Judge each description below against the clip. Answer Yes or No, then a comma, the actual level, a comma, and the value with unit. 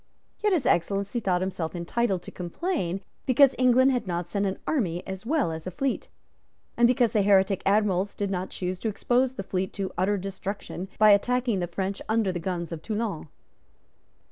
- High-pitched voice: Yes, high, 195 Hz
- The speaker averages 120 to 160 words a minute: No, average, 185 wpm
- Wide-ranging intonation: No, average, 4.4 semitones